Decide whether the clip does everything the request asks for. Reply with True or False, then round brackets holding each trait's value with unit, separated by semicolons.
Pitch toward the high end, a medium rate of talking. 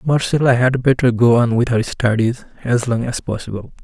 False (120 Hz; 190 wpm)